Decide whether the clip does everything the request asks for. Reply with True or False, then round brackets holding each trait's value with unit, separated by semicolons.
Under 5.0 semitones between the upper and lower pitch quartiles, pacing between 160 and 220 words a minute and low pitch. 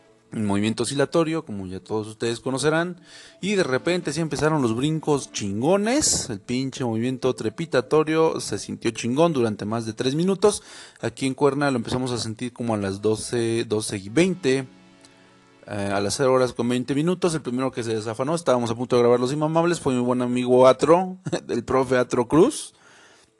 False (5.4 semitones; 180 wpm; 125 Hz)